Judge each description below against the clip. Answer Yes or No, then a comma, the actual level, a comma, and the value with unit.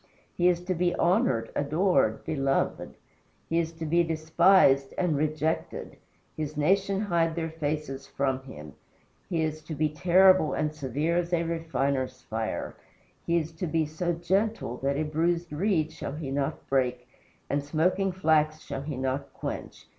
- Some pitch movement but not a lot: Yes, average, 3.6 semitones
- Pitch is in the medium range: Yes, medium, 155 Hz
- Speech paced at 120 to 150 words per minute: No, average, 160 wpm